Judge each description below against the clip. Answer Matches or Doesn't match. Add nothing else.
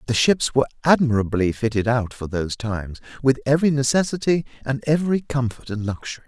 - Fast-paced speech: Doesn't match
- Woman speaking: Doesn't match